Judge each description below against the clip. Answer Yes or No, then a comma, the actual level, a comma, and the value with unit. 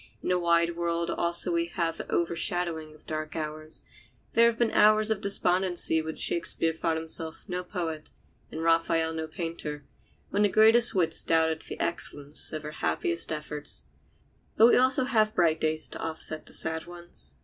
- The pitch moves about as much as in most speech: No, narrow, 2.1 semitones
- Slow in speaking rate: No, average, 170 wpm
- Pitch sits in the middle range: Yes, medium, 165 Hz